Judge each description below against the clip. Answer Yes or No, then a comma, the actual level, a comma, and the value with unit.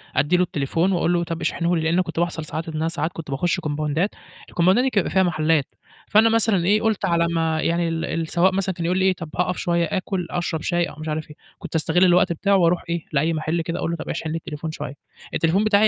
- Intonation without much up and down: Yes, narrow, 2.2 semitones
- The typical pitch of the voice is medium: Yes, medium, 170 Hz